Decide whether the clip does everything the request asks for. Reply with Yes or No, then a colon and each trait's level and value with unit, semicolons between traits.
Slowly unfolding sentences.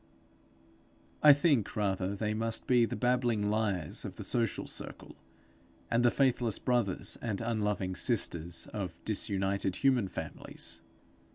Yes: slow, 125 wpm